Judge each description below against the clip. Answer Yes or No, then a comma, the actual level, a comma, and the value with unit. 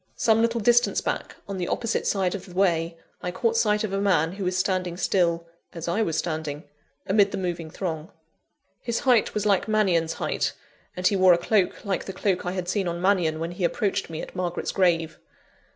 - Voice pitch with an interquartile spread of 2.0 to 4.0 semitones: Yes, average, 2.9 semitones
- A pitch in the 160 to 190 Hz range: Yes, medium, 185 Hz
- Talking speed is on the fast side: Yes, fast, 210 wpm